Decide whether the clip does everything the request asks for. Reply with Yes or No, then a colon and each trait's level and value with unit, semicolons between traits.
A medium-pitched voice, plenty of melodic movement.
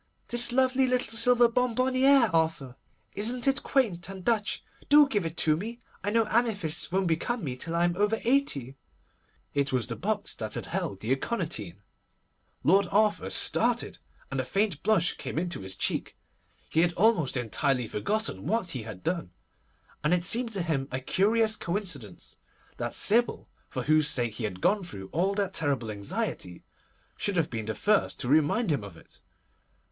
Yes: medium, 175 Hz; wide, 8.6 semitones